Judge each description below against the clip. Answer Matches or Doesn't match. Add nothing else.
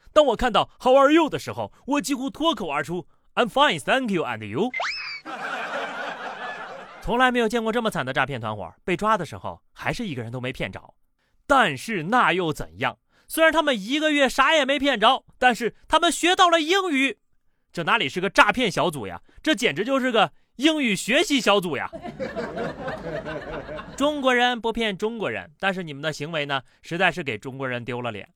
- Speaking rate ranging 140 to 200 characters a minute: Doesn't match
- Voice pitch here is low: Doesn't match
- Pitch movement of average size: Doesn't match